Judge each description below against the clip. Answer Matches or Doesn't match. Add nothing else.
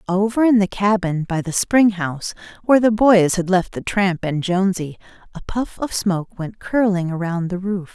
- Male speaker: Doesn't match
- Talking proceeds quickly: Doesn't match